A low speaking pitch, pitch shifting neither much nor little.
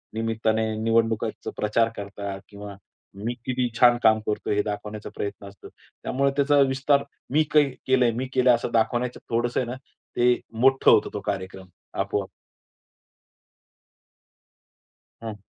Yes: low, 115 Hz; average, 3.5 semitones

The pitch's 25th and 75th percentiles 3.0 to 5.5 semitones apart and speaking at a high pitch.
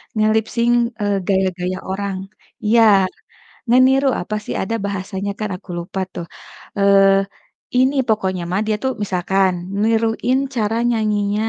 No: narrow, 2.6 semitones; high, 205 Hz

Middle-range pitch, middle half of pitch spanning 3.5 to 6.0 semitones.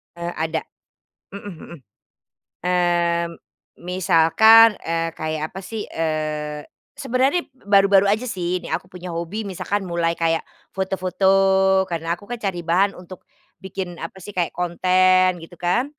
No: medium, 180 Hz; narrow, 2.6 semitones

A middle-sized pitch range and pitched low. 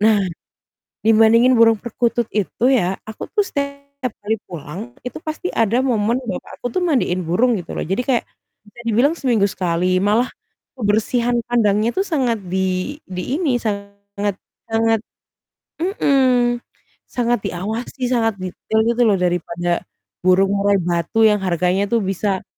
No: average, 3.8 semitones; high, 220 Hz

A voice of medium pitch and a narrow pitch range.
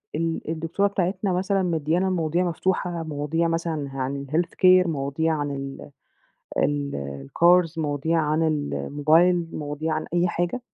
No: medium, 160 Hz; average, 3.2 semitones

